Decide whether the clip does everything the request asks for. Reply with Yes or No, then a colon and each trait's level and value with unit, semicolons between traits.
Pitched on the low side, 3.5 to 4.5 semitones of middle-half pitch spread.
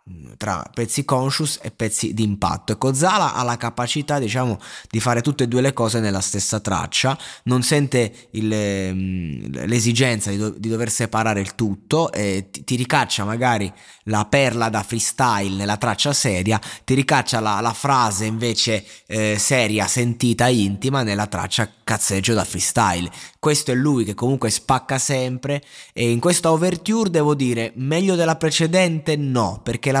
Yes: low, 120 Hz; average, 4.0 semitones